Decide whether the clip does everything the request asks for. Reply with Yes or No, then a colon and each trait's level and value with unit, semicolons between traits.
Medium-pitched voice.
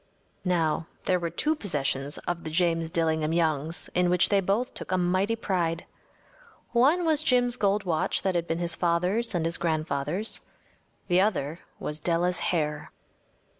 Yes: medium, 175 Hz